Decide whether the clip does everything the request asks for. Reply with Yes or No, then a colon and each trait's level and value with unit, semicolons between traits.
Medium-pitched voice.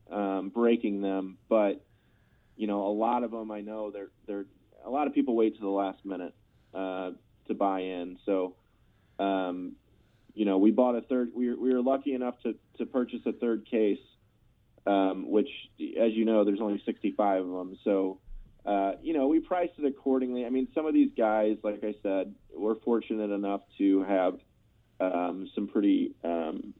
No: low, 105 Hz